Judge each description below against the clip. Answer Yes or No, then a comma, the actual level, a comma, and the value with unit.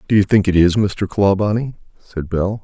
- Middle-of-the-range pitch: No, low, 100 Hz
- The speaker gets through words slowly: No, fast, 205 wpm